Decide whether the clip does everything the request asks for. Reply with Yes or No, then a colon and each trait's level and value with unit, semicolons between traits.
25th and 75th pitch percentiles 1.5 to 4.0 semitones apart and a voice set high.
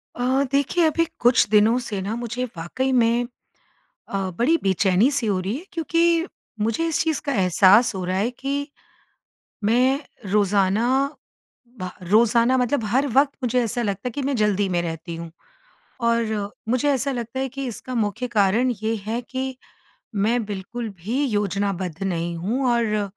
No: average, 4.5 semitones; high, 230 Hz